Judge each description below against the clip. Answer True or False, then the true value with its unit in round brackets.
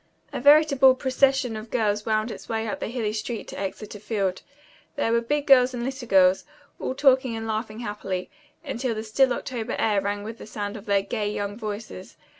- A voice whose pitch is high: True (225 Hz)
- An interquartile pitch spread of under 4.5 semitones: True (3.6 semitones)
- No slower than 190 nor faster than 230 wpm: True (200 wpm)